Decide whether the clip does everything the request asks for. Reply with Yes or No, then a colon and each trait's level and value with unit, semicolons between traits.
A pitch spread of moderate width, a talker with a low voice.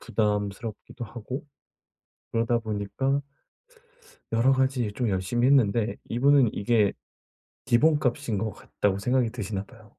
Yes: average, 3.8 semitones; low, 115 Hz